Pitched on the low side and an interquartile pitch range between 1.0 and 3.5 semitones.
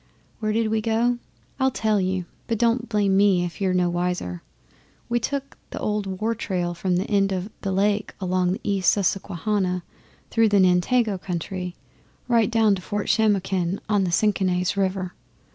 No: high, 195 Hz; average, 3.0 semitones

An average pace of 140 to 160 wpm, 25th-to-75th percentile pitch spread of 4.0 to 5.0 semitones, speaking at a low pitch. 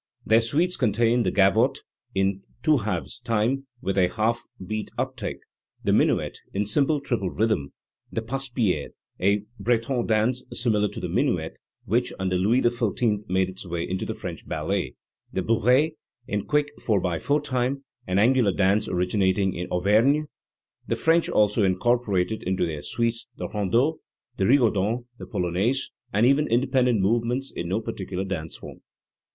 Yes: average, 155 wpm; average, 4.3 semitones; low, 110 Hz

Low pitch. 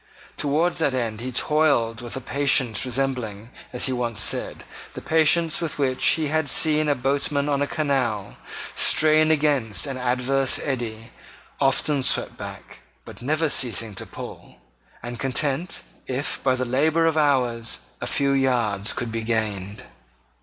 Yes: low, 130 Hz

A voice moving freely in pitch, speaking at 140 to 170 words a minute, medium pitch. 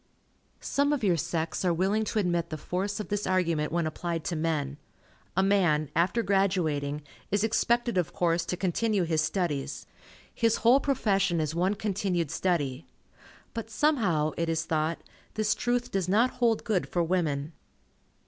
No: average, 4.4 semitones; average, 160 wpm; medium, 180 Hz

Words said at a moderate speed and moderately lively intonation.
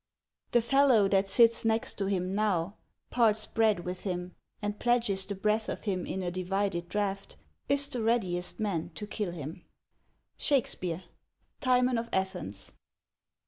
Yes: average, 150 wpm; average, 3.8 semitones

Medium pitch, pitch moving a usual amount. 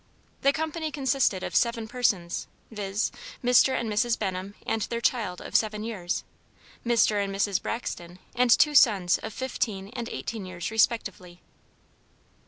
No: high, 220 Hz; average, 3.8 semitones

